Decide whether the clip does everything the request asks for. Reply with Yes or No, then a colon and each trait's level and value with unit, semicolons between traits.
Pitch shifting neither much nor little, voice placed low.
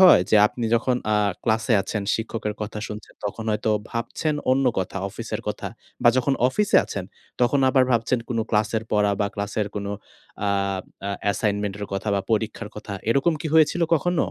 Yes: average, 3.8 semitones; low, 110 Hz